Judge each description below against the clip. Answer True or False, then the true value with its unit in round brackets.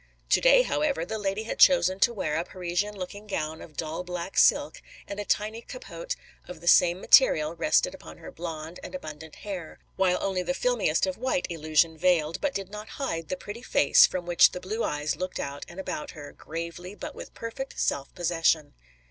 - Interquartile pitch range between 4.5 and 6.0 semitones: True (4.8 semitones)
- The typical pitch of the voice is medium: True (180 Hz)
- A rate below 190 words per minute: False (200 wpm)